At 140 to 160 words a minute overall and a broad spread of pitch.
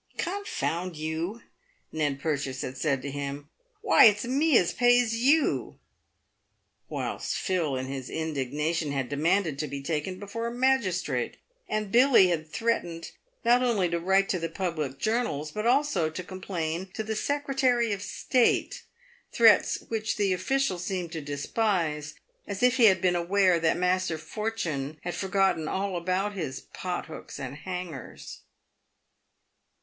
Yes: average, 150 wpm; wide, 6.1 semitones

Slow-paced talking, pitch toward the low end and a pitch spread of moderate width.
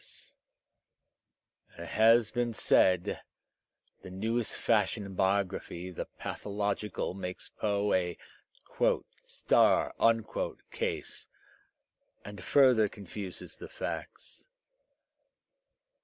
Yes: slow, 80 wpm; low, 100 Hz; average, 3.0 semitones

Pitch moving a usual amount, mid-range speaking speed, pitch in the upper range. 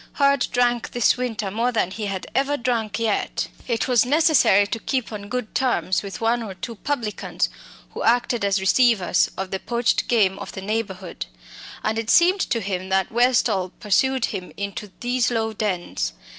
Yes: average, 3.8 semitones; average, 175 wpm; high, 225 Hz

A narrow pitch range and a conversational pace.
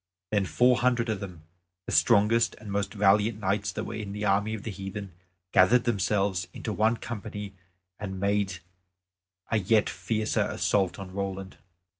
Yes: narrow, 2.0 semitones; average, 160 wpm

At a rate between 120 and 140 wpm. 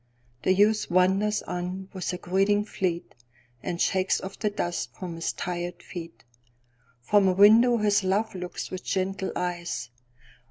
Yes: slow, 135 wpm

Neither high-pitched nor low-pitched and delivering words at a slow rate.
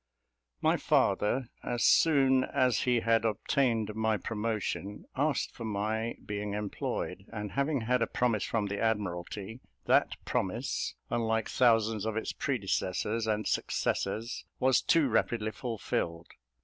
No: low, 110 Hz; slow, 130 wpm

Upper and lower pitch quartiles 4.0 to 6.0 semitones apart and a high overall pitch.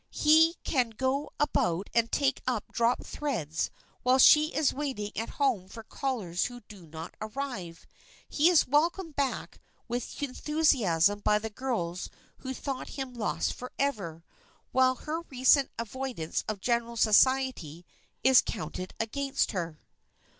Yes: average, 5.1 semitones; high, 245 Hz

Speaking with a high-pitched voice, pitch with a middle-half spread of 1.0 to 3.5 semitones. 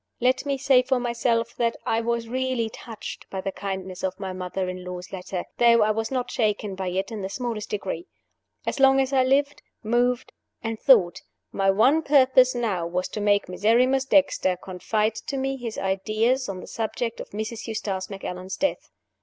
No: high, 225 Hz; average, 4.8 semitones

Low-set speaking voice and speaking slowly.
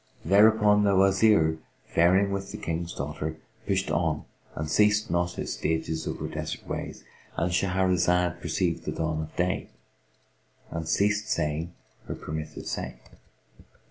Yes: very low, 90 Hz; slow, 130 wpm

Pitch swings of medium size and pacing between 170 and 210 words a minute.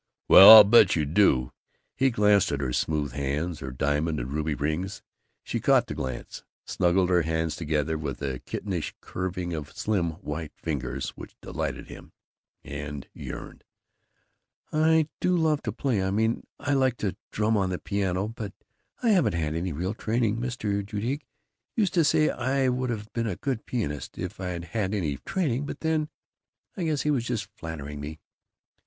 No: wide, 7.4 semitones; average, 175 wpm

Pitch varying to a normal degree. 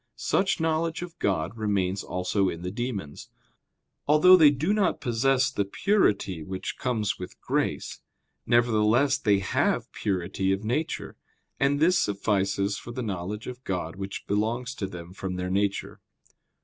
No: wide, 5.9 semitones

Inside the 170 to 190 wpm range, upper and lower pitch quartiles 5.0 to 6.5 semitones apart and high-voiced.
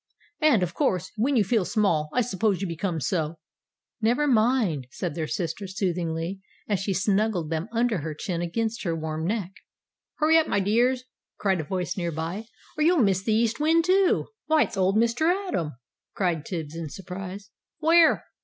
Yes: average, 180 wpm; wide, 5.6 semitones; high, 195 Hz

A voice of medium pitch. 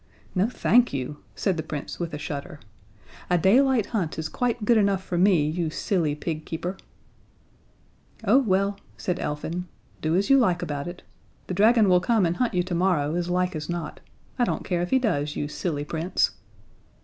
Yes: medium, 180 Hz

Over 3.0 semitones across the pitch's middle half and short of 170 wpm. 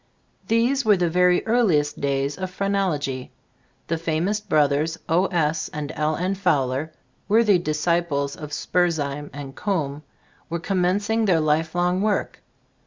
Yes: average, 4.4 semitones; slow, 135 wpm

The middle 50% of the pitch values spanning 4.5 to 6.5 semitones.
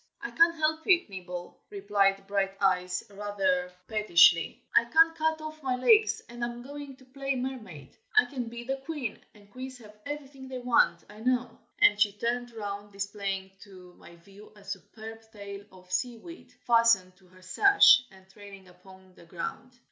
Yes: average, 5.2 semitones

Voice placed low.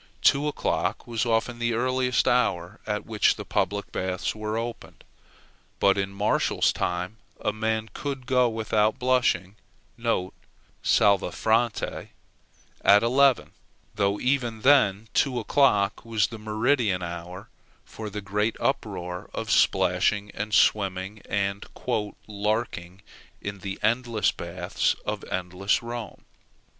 Yes: low, 110 Hz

